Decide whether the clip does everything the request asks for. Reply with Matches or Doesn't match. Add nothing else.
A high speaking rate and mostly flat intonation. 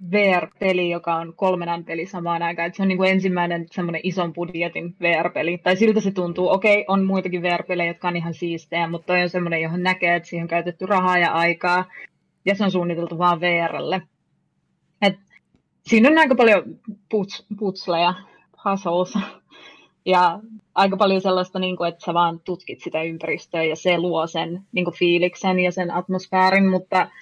Matches